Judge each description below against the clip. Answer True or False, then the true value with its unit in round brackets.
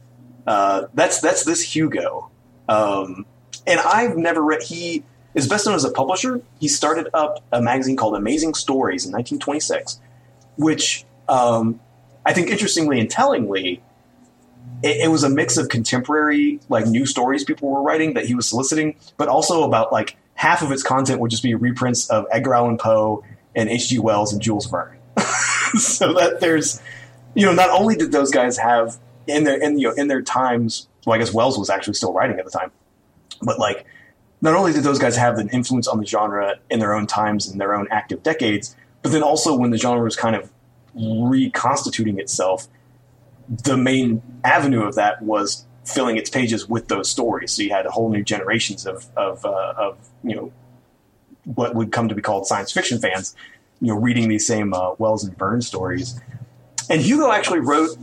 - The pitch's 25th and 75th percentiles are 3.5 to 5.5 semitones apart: True (4.5 semitones)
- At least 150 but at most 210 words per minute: True (190 wpm)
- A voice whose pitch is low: True (120 Hz)